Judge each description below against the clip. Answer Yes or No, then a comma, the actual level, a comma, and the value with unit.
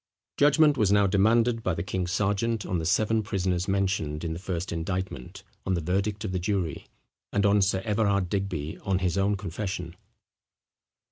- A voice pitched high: No, very low, 95 Hz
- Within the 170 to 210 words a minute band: Yes, average, 175 wpm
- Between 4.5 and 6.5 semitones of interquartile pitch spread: No, narrow, 2.5 semitones